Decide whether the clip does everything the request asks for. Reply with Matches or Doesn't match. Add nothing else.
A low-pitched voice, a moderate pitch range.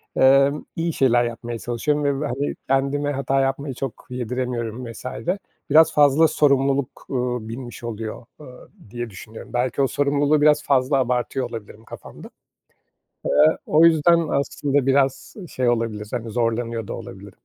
Matches